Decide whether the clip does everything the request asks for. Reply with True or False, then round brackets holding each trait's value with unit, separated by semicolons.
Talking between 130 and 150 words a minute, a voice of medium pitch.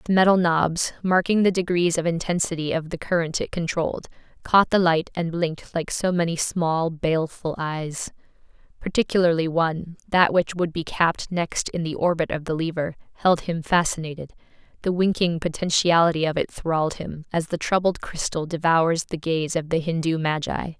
False (170 wpm; 165 Hz)